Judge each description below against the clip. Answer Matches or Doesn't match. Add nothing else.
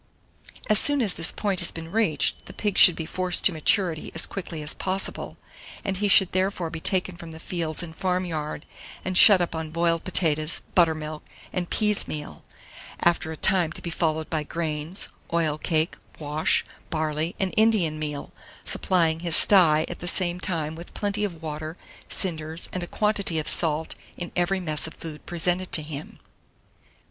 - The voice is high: Doesn't match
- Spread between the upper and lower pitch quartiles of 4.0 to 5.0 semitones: Doesn't match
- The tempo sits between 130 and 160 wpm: Doesn't match